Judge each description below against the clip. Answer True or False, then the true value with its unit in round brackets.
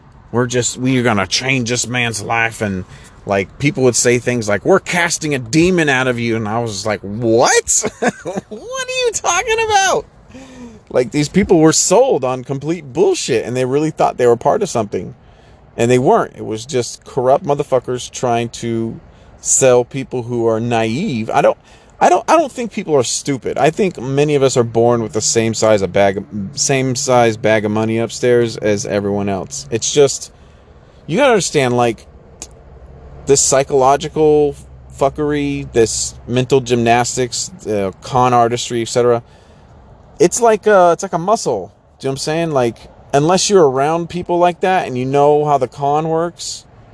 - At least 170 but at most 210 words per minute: True (180 wpm)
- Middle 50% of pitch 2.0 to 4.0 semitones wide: False (4.6 semitones)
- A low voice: True (125 Hz)